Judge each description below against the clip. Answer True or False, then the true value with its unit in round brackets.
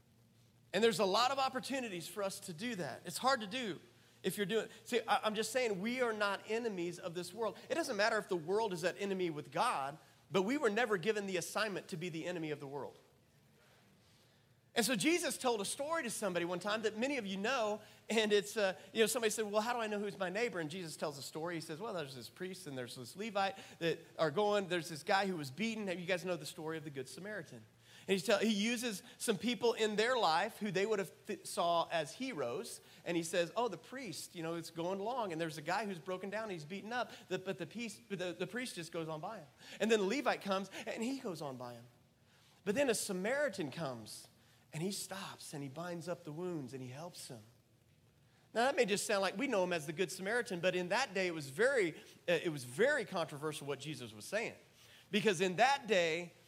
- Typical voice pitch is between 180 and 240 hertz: True (190 Hz)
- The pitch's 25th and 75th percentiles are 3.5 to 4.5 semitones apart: False (5.1 semitones)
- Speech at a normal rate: False (245 wpm)